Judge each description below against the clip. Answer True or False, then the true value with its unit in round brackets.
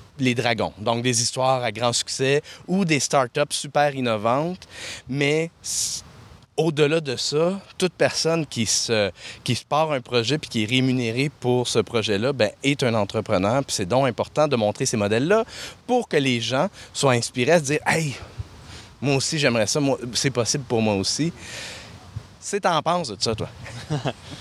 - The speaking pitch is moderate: False (130 Hz)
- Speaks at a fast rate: False (170 wpm)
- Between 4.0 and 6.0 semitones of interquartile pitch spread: True (4.5 semitones)